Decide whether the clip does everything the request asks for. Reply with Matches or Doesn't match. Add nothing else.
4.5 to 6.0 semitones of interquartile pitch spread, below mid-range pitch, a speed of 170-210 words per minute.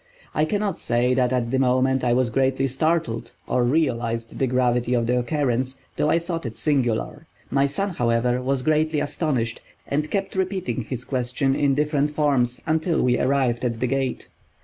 Doesn't match